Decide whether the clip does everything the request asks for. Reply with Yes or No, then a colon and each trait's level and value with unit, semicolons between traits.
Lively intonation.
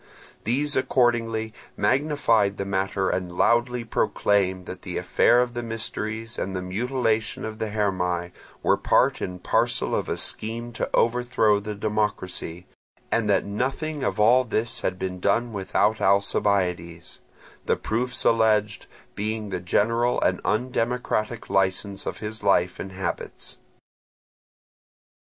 No: average, 3.5 semitones